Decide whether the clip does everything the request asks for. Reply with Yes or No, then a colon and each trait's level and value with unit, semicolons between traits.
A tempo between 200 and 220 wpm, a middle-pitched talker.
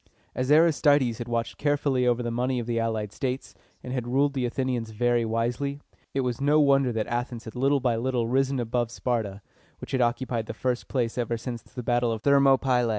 No: fast, 205 wpm; low, 125 Hz